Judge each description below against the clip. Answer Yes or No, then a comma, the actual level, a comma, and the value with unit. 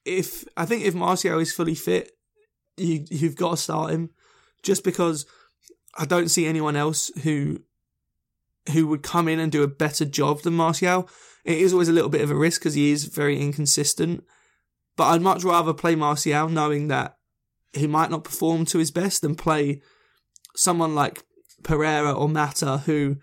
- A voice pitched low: No, medium, 160 Hz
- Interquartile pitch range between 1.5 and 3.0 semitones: Yes, narrow, 2.4 semitones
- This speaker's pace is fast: No, average, 180 wpm